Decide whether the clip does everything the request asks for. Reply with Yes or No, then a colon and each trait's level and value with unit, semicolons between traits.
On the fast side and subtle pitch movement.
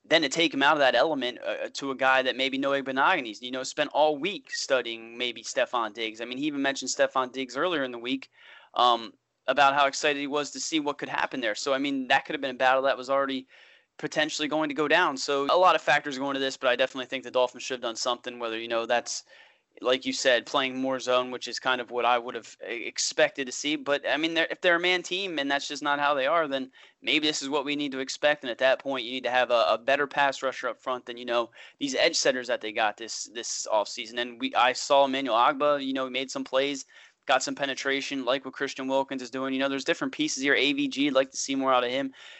Yes: fast, 275 wpm; narrow, 2.2 semitones